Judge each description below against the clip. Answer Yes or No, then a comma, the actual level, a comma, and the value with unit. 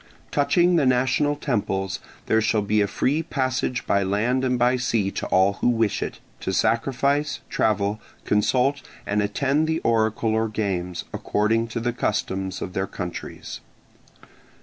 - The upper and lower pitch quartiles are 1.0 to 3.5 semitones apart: No, average, 4.3 semitones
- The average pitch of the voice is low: Yes, low, 115 Hz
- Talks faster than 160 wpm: No, average, 150 wpm